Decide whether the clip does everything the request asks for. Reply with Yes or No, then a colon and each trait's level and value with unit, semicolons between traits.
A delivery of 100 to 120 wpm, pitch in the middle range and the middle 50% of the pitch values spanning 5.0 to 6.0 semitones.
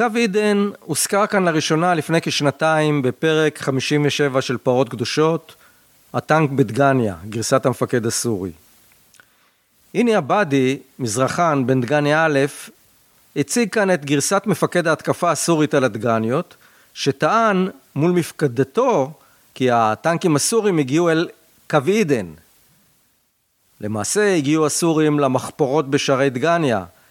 No: average, 105 wpm; medium, 150 Hz; average, 4.3 semitones